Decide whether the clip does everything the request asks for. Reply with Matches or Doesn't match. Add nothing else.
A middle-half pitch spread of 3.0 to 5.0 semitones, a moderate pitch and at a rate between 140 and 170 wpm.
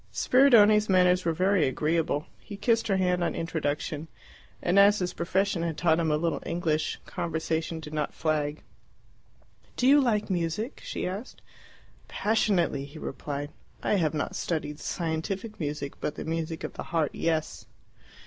Matches